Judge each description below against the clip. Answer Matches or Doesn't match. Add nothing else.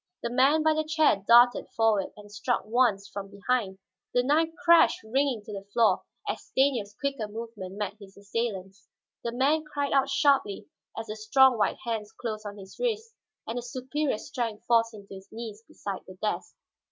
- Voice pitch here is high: Matches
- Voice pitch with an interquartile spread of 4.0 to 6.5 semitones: Matches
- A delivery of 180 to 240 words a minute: Matches